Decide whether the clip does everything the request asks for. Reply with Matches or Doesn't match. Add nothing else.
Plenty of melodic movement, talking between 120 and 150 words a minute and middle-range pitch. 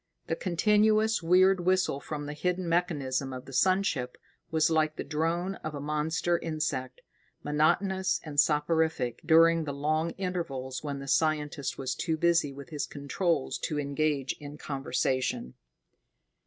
Doesn't match